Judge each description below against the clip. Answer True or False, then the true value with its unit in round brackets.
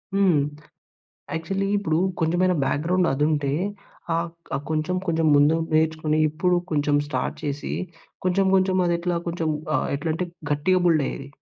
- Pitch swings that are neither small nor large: True (3.3 semitones)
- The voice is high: False (160 Hz)